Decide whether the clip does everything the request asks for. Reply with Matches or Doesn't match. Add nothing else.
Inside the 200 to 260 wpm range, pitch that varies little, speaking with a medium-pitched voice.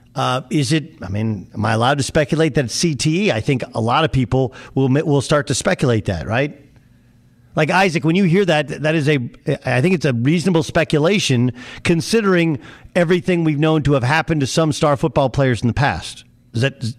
Doesn't match